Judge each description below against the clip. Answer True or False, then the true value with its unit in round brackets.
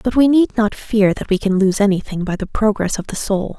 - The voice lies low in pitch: False (205 Hz)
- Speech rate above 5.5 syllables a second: False (5.4 syllables/s)